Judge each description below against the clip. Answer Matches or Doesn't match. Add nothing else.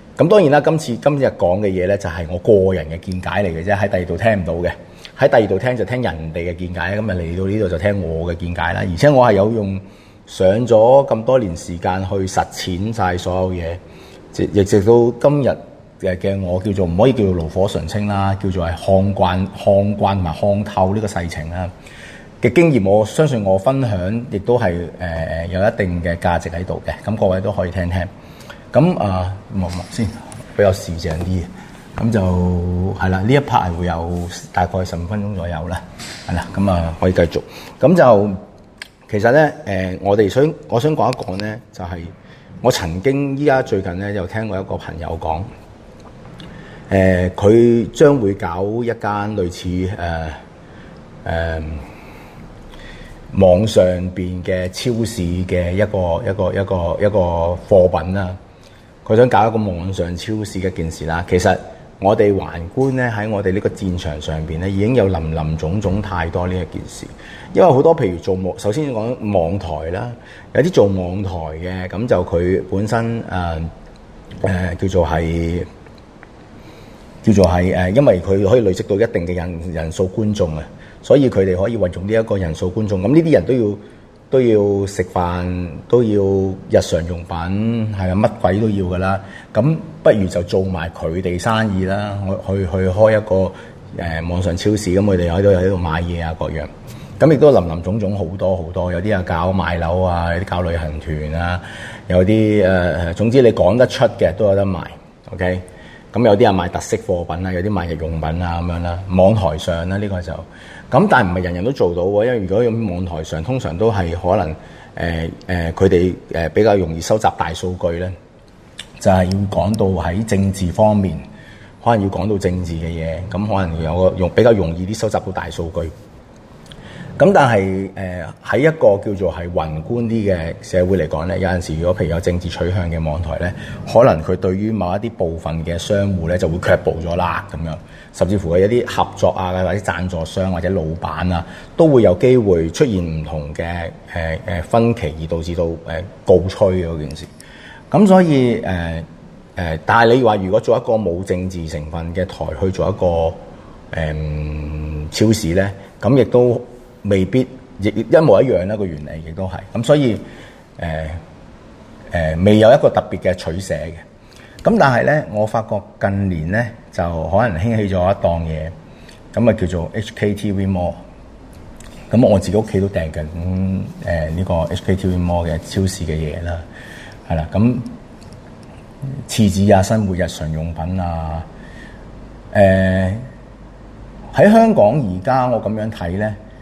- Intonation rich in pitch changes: Doesn't match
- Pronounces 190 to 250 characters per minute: Doesn't match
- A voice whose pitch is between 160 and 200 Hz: Doesn't match